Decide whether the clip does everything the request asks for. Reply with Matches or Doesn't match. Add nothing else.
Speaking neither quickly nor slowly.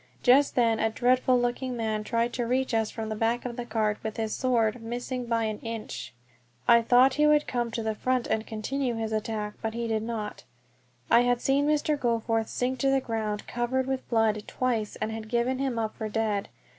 Doesn't match